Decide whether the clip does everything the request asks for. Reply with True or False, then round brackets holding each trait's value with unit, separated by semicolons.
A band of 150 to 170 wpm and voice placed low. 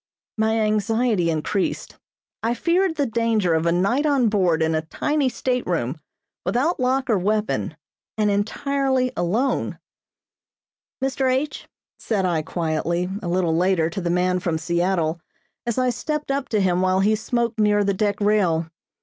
False (160 wpm; 205 Hz)